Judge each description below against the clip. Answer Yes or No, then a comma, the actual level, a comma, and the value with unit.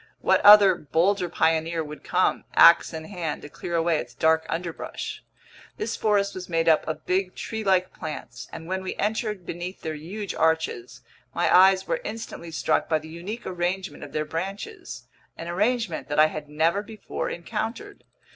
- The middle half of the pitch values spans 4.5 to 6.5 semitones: No, average, 3.8 semitones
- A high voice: No, medium, 175 Hz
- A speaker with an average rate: Yes, average, 165 wpm